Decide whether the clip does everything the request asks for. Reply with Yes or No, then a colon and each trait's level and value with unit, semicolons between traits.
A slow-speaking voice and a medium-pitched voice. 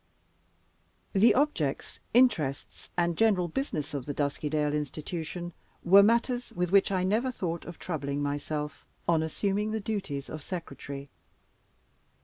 Yes: slow, 130 wpm; medium, 170 Hz